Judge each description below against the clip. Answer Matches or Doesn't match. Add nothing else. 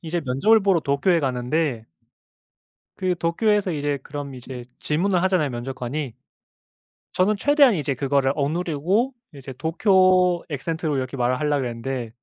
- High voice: Doesn't match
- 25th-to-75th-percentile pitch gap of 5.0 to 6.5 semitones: Matches